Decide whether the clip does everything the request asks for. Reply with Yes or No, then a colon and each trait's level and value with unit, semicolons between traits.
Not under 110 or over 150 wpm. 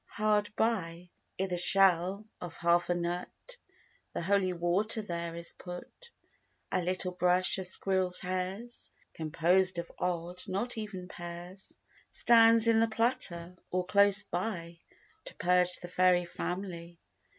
Yes: slow, 135 wpm